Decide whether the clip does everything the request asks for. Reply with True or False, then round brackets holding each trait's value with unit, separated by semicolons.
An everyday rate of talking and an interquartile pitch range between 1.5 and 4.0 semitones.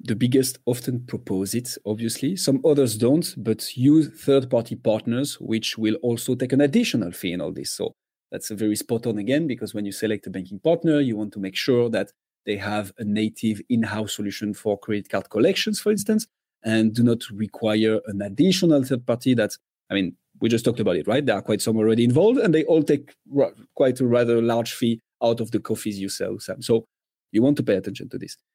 False (215 wpm; 3.6 semitones)